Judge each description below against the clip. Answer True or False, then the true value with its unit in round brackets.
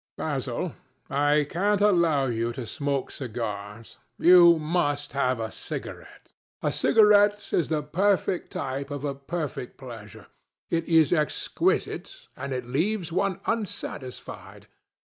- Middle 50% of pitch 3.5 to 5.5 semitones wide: True (5.2 semitones)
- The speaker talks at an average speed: False (125 wpm)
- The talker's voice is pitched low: False (145 Hz)